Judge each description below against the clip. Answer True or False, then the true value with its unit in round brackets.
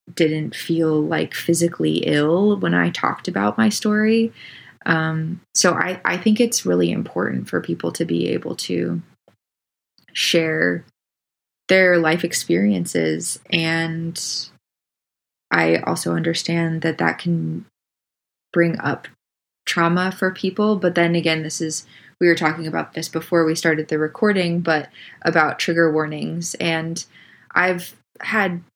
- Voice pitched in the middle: True (165 Hz)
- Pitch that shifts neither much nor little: False (2.3 semitones)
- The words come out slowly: True (130 wpm)